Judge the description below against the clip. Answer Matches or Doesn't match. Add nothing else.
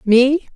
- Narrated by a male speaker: Doesn't match